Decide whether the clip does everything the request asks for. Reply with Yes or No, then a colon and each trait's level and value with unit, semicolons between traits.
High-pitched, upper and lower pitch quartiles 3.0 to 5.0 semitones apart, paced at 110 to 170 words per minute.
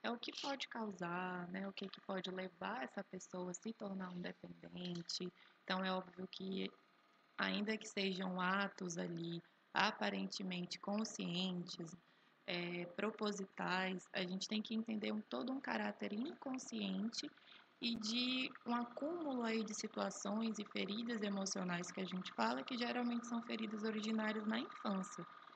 Yes: high, 200 Hz; average, 3.4 semitones; average, 145 wpm